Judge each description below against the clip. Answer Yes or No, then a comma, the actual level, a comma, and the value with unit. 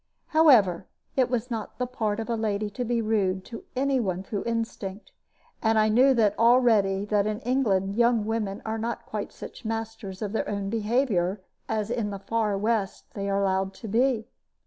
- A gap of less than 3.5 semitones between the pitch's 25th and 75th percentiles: Yes, average, 2.8 semitones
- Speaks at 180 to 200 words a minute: Yes, average, 185 wpm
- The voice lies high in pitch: Yes, high, 220 Hz